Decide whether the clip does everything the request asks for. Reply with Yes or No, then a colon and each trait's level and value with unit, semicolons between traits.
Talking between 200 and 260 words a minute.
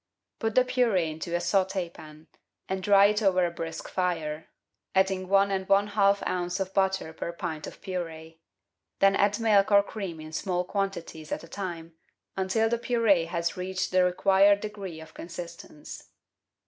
No: average, 165 wpm